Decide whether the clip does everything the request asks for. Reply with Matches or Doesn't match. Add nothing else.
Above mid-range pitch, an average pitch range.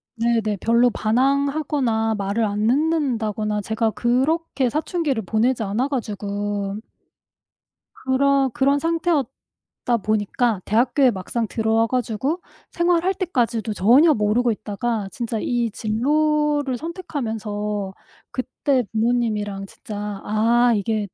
Matches